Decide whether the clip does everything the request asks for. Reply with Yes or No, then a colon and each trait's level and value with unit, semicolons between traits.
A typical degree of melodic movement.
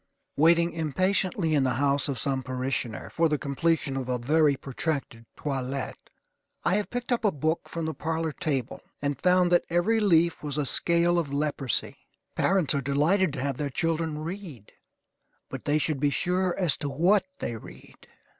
Yes: average, 3.8 semitones